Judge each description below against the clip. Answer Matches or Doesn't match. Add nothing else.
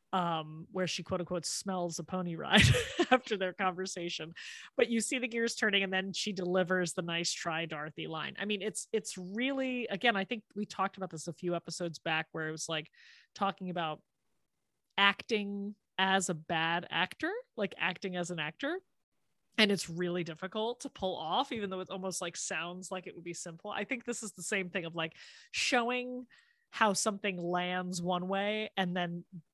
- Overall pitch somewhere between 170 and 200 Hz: Matches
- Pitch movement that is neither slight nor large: Matches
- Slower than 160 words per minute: Doesn't match